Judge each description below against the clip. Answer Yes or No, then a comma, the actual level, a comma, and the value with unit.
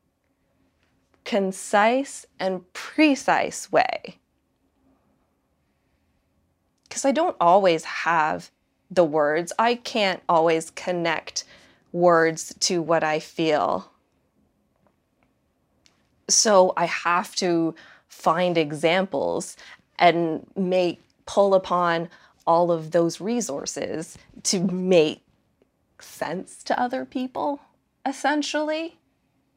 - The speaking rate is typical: No, slow, 85 wpm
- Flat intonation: No, average, 4.7 semitones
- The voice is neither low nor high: Yes, medium, 175 Hz